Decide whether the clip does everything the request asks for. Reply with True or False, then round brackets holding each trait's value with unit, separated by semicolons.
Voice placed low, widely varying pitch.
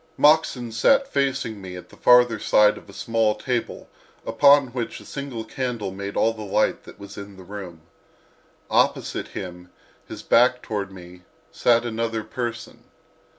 False (115 Hz; 3.7 semitones)